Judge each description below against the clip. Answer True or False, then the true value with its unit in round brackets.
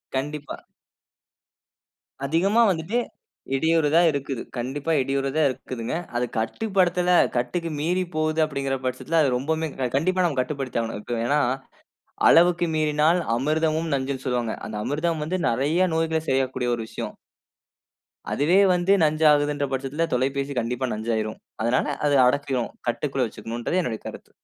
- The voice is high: False (145 Hz)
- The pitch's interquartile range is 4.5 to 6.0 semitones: False (4.1 semitones)